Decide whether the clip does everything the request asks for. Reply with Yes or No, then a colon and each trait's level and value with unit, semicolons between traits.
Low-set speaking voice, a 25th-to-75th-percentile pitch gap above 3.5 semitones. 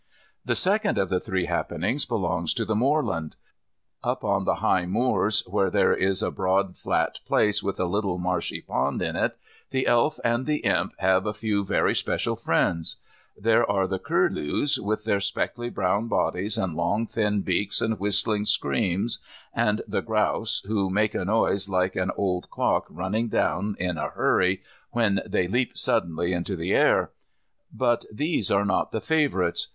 No: low, 100 Hz; average, 3.1 semitones